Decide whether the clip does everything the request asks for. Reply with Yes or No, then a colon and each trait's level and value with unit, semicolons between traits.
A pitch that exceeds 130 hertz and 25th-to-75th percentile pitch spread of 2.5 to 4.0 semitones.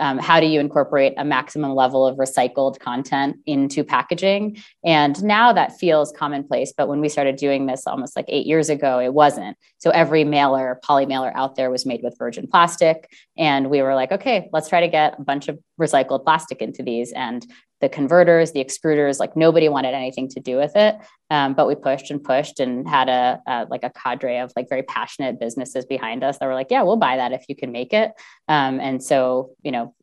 Yes: medium, 140 Hz; average, 3.2 semitones